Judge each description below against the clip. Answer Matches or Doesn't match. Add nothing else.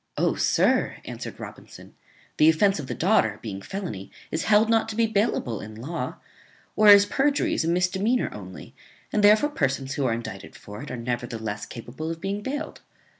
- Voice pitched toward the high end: Doesn't match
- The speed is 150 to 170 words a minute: Doesn't match